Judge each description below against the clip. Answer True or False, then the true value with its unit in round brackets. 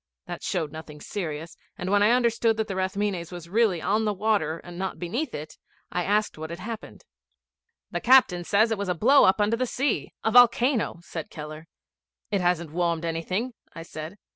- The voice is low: False (190 Hz)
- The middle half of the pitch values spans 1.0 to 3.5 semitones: False (4.8 semitones)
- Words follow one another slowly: False (190 wpm)